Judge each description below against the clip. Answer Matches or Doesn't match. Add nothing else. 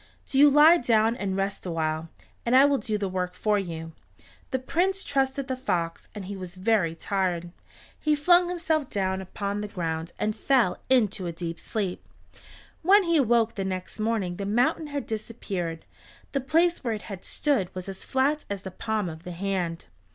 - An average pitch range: Doesn't match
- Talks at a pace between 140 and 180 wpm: Doesn't match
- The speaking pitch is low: Doesn't match